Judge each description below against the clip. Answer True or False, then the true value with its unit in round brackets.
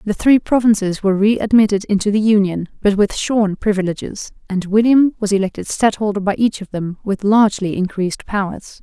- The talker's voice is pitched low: False (205 Hz)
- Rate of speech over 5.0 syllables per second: True (5.5 syllables/s)